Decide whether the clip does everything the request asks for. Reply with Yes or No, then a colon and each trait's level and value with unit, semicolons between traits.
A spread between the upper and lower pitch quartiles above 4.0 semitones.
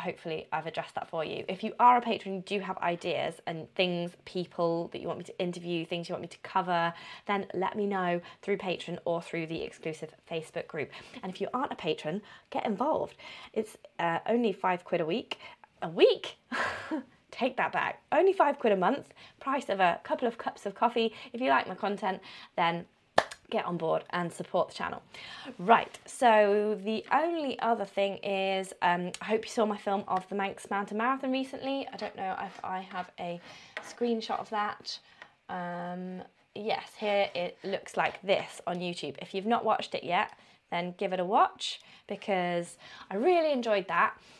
Yes: average, 4.6 semitones